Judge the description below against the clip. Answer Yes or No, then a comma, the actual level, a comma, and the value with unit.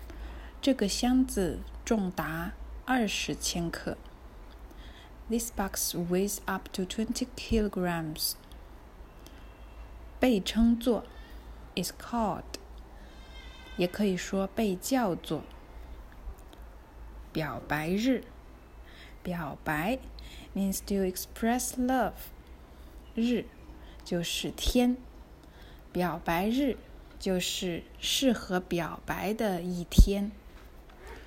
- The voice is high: No, medium, 180 Hz